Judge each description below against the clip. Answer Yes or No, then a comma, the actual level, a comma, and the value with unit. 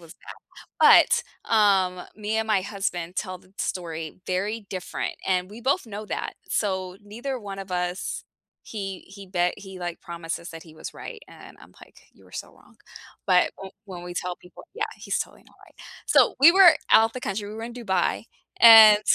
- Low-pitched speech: No, high, 195 Hz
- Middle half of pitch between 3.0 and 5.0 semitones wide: Yes, average, 3.4 semitones